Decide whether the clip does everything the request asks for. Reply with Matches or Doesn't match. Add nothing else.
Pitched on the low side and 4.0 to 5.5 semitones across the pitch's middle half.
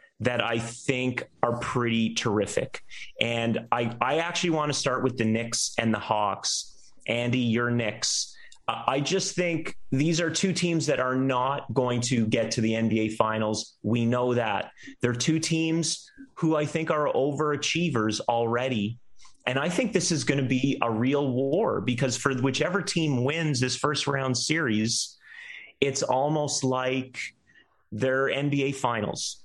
Matches